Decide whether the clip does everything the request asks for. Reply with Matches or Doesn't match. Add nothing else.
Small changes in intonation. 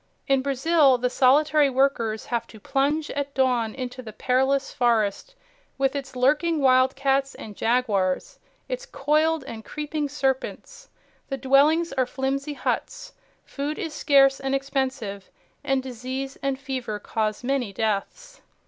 Matches